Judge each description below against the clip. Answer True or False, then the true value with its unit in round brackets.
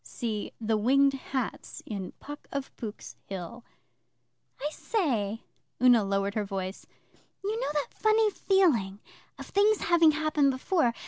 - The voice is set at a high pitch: True (260 Hz)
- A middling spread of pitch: False (7.0 semitones)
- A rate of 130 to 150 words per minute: True (135 wpm)